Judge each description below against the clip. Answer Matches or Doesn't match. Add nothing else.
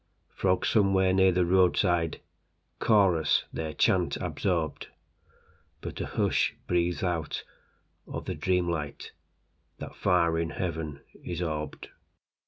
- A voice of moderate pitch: Doesn't match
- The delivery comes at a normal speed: Doesn't match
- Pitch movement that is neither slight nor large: Doesn't match